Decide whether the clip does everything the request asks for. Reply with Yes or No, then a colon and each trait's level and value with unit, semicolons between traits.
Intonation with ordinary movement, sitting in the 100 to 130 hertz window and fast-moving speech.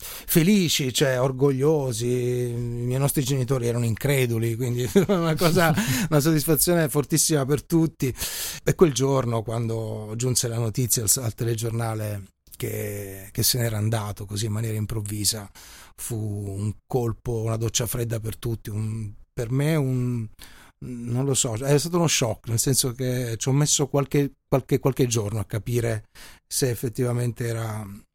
No: average, 3.6 semitones; low, 120 Hz; average, 145 wpm